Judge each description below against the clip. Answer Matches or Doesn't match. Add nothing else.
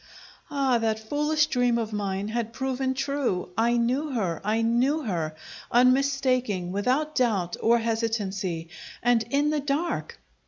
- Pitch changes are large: Doesn't match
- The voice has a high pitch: Matches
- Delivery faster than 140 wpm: Doesn't match